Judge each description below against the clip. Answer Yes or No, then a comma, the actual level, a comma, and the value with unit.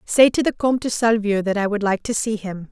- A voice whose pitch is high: Yes, high, 215 Hz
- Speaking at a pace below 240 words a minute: No, fast, 290 wpm